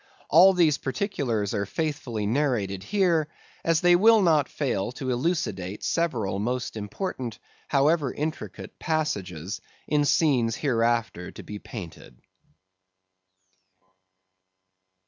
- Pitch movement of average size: No, wide, 7.2 semitones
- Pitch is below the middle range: Yes, low, 130 Hz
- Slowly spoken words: Yes, slow, 105 wpm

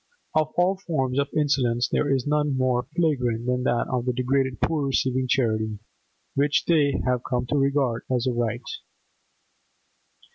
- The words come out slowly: No, average, 155 wpm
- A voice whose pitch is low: Yes, low, 130 Hz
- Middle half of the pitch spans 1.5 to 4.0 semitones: Yes, average, 2.8 semitones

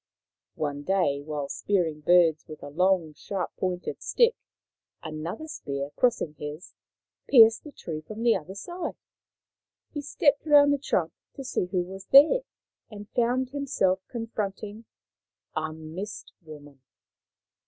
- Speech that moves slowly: Yes, slow, 130 wpm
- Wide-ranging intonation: Yes, wide, 7.5 semitones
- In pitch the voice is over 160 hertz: Yes, high, 190 Hz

